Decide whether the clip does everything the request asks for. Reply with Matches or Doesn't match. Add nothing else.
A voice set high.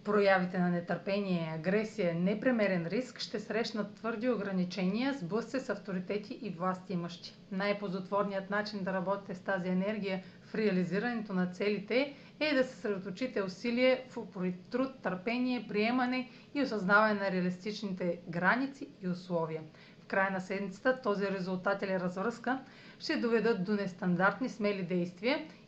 Matches